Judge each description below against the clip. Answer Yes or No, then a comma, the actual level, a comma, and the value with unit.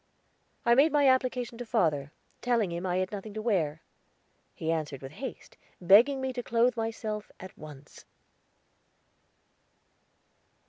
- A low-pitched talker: No, high, 215 Hz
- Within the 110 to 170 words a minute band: Yes, slow, 135 wpm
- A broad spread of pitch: Yes, wide, 6.6 semitones